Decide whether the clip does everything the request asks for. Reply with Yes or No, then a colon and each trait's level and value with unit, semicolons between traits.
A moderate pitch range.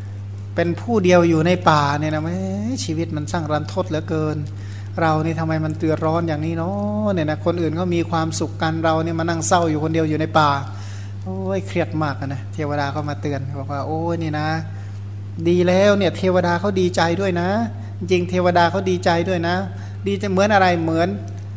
No: wide, 8.3 semitones